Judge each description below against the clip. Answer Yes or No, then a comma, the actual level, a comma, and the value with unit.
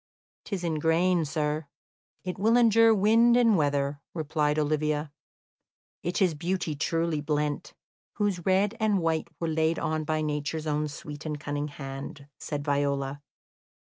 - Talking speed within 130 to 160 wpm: Yes, average, 140 wpm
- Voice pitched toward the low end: No, medium, 155 Hz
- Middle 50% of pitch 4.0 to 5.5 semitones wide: No, average, 3.5 semitones